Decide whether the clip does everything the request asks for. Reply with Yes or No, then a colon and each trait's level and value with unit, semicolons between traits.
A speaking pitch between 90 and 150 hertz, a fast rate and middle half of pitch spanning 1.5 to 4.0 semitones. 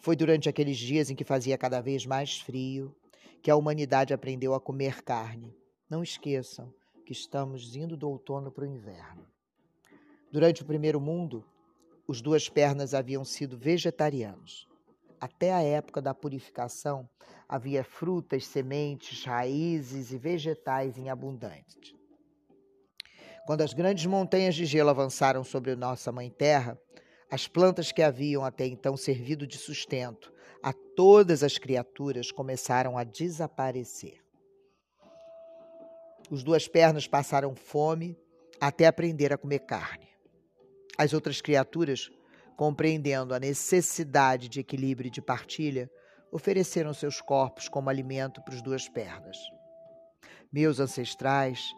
No: medium, 140 Hz; average, 125 wpm; average, 3.5 semitones